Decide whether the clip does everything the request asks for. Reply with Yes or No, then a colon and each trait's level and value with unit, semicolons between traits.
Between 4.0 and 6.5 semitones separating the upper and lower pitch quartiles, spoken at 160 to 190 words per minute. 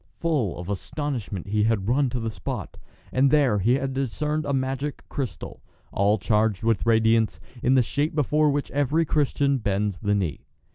Yes: average, 5.3 semitones; average, 175 wpm